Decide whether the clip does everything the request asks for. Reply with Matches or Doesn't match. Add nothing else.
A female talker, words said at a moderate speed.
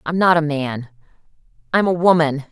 Matches